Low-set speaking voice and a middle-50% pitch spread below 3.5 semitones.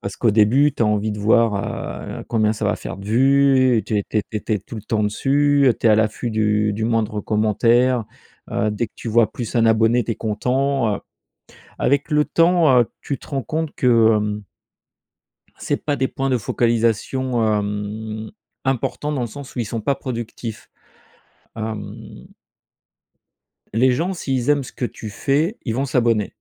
No: low, 115 Hz; average, 3.8 semitones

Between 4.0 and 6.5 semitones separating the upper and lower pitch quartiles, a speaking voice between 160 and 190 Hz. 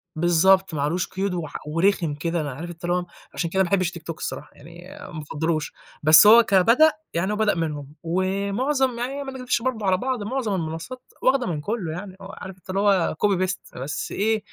Yes: average, 4.3 semitones; medium, 185 Hz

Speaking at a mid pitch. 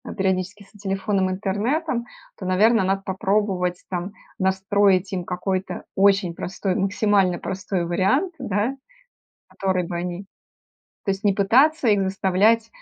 No: high, 195 Hz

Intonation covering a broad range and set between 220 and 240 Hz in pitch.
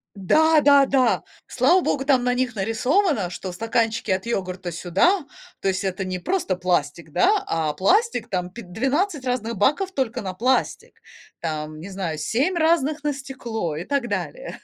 Yes: wide, 7.6 semitones; high, 230 Hz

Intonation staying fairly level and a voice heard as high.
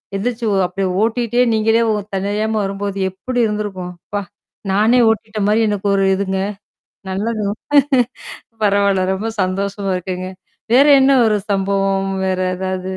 Yes: narrow, 2.3 semitones; high, 200 Hz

